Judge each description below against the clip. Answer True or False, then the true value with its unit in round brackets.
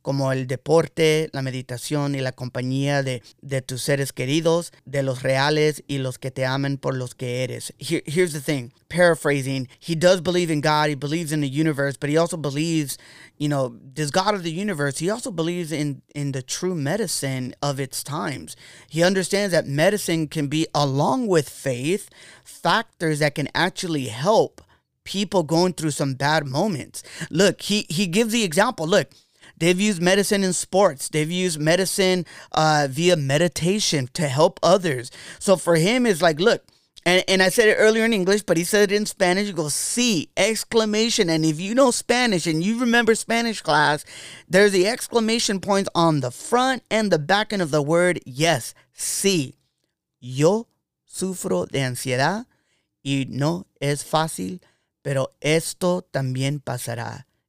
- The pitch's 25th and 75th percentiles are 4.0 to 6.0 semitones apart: True (5.1 semitones)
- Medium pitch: True (160 Hz)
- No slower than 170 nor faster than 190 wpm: True (175 wpm)